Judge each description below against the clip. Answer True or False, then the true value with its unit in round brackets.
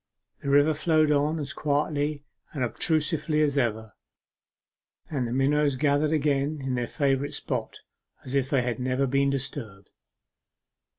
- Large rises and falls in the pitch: False (2.5 semitones)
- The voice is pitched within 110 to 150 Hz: True (140 Hz)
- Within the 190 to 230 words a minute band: False (140 wpm)